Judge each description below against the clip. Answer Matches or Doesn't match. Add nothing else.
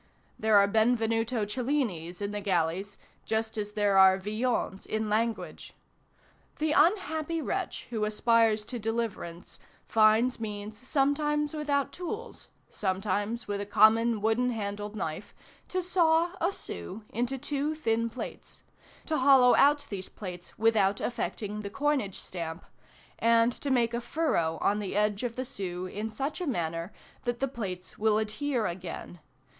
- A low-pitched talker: Doesn't match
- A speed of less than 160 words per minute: Matches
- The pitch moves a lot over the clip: Doesn't match